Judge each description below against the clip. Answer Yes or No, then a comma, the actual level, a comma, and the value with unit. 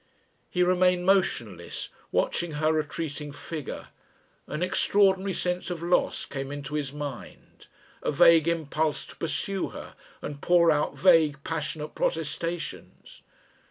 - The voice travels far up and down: No, average, 3.2 semitones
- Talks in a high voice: No, medium, 160 Hz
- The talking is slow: Yes, slow, 125 wpm